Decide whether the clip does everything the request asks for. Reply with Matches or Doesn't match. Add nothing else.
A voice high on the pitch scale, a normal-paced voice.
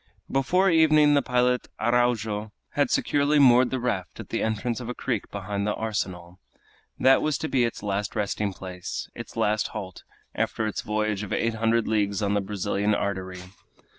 Doesn't match